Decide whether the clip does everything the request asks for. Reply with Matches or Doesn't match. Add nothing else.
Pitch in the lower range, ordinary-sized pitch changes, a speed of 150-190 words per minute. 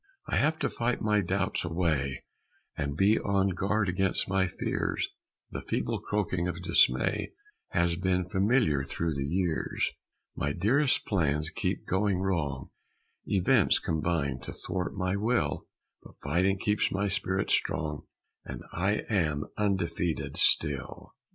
Doesn't match